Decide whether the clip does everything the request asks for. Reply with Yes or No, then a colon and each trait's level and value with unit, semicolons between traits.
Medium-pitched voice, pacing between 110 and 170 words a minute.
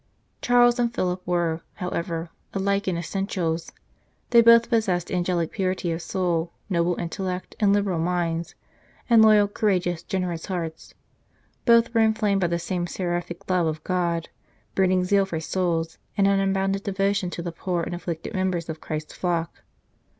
Yes: medium, 180 Hz; average, 155 wpm